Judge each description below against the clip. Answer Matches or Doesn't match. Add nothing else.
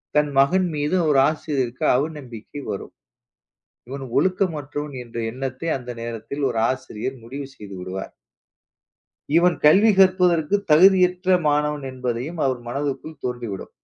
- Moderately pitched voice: Matches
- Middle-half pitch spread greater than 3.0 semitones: Matches